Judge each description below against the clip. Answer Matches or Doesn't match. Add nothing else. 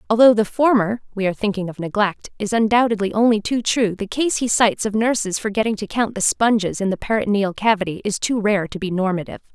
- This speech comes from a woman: Matches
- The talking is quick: Matches